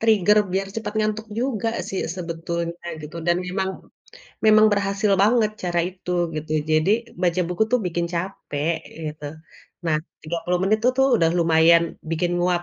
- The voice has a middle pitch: Yes, medium, 180 Hz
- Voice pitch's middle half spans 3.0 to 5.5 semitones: Yes, average, 3.8 semitones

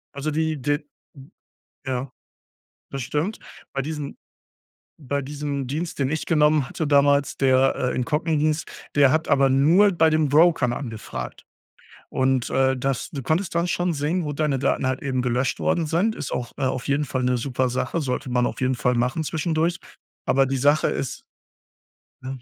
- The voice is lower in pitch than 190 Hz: Yes, medium, 140 Hz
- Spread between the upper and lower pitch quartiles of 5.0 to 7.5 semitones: No, average, 3.2 semitones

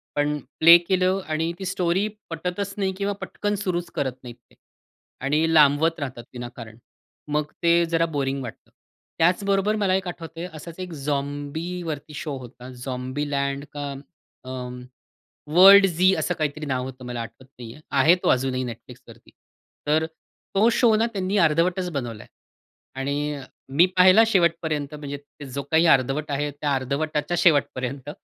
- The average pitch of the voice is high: No, medium, 150 Hz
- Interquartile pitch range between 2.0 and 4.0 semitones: No, average, 4.4 semitones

